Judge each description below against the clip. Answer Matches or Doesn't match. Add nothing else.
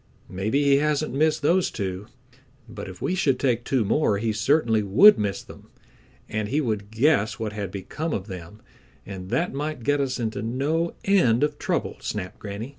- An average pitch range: Doesn't match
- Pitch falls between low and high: Doesn't match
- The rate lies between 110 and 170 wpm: Doesn't match